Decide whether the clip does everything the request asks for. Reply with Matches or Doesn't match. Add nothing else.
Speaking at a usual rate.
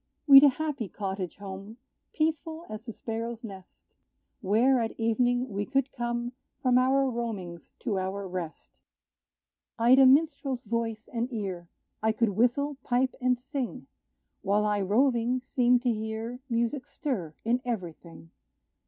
Matches